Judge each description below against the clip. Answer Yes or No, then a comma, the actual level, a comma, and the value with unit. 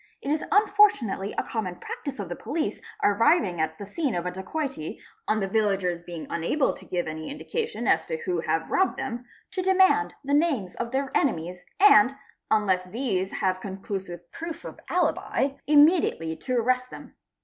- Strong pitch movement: Yes, wide, 8.4 semitones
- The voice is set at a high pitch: Yes, high, 220 Hz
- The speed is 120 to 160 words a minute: No, average, 175 wpm